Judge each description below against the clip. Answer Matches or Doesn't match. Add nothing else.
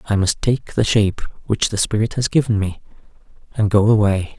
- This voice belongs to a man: Matches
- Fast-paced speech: Doesn't match